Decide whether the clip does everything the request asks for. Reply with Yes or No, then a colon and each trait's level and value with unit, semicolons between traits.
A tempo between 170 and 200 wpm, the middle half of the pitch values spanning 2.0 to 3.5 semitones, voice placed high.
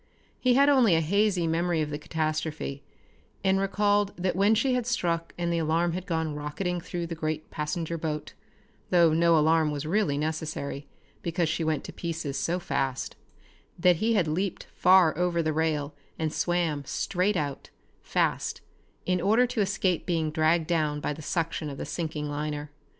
No: average, 175 wpm; average, 2.9 semitones; medium, 165 Hz